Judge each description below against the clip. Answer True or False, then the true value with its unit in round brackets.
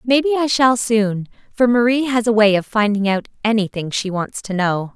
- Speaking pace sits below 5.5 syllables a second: True (5.0 syllables/s)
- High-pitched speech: True (220 Hz)